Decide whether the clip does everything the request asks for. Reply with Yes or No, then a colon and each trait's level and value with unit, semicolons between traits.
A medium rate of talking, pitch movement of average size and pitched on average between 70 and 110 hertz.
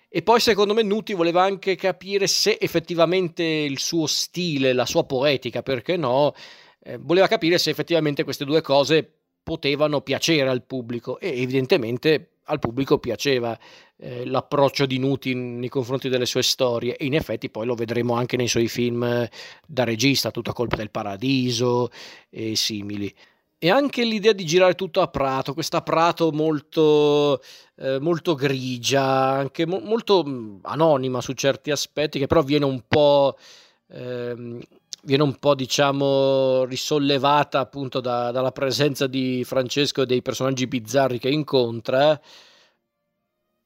No: average, 145 wpm; average, 4.1 semitones; low, 135 Hz